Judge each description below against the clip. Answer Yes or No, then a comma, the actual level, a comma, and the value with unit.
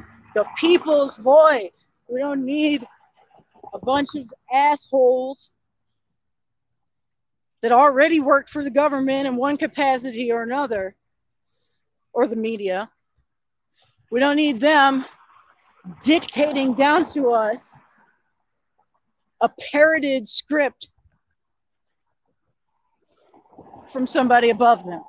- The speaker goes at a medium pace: No, slow, 95 wpm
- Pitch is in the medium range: No, very high, 275 Hz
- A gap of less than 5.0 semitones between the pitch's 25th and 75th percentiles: Yes, average, 3.5 semitones